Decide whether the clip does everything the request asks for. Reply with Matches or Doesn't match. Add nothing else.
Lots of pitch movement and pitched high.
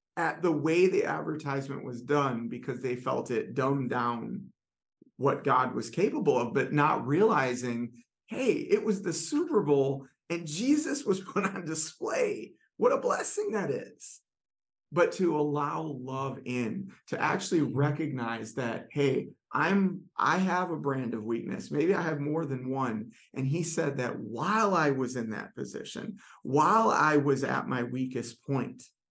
Doesn't match